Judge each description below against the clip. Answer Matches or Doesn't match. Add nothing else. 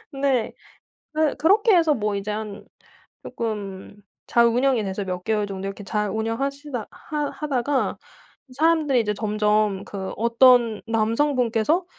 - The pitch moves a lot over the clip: Doesn't match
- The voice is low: Doesn't match